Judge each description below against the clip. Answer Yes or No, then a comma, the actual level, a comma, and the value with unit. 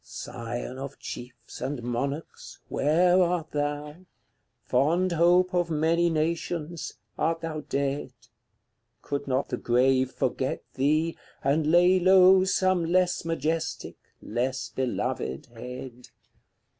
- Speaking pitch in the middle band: Yes, medium, 155 Hz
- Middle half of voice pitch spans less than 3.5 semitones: No, average, 4.7 semitones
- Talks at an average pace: No, slow, 115 wpm